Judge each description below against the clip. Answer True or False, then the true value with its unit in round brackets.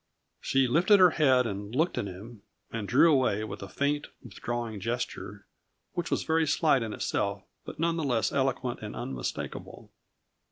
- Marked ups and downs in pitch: True (6.0 semitones)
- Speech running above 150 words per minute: True (165 wpm)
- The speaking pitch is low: True (125 Hz)